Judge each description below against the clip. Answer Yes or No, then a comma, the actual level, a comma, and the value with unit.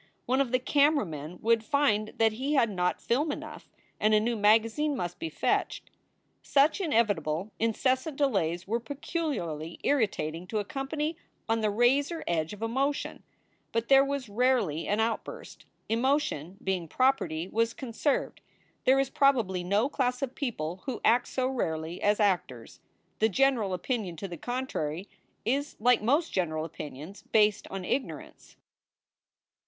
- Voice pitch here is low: No, high, 225 Hz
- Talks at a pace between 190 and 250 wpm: No, average, 150 wpm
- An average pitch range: No, wide, 6.5 semitones